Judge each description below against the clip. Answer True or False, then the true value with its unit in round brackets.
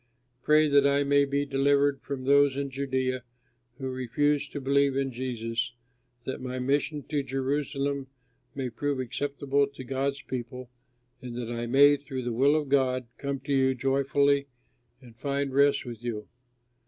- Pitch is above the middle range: False (135 Hz)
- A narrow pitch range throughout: True (1.7 semitones)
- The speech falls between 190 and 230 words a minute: False (160 wpm)